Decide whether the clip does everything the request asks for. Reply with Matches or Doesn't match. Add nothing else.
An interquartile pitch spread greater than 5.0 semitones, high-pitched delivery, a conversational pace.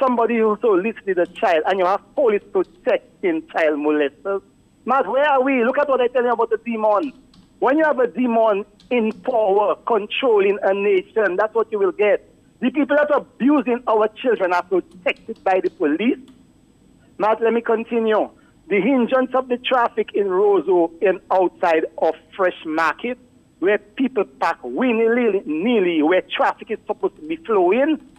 Matches